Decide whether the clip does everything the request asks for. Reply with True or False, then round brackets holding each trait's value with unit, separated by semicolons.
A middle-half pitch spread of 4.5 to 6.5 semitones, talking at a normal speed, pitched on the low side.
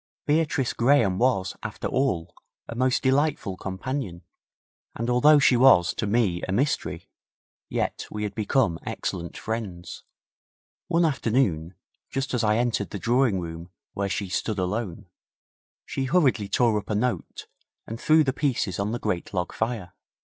True (5.5 semitones; 150 wpm; 115 Hz)